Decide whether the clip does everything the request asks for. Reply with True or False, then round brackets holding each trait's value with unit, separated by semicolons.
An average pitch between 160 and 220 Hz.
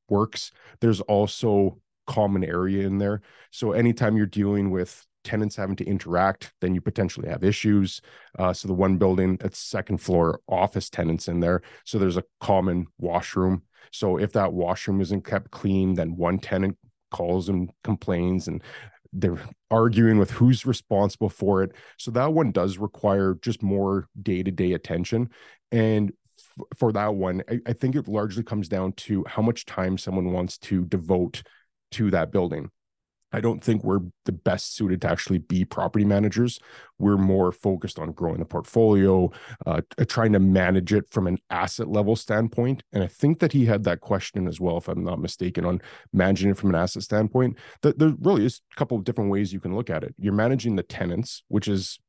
False (100 Hz)